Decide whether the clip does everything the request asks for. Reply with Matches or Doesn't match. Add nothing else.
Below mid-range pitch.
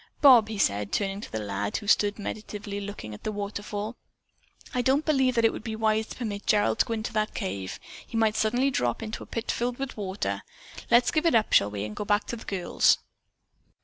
Doesn't match